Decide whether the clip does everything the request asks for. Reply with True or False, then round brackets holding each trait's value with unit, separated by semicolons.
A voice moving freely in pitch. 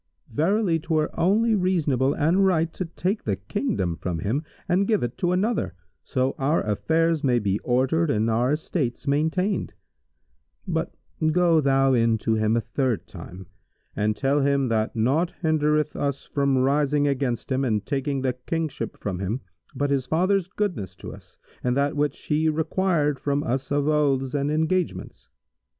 False (4.7 semitones)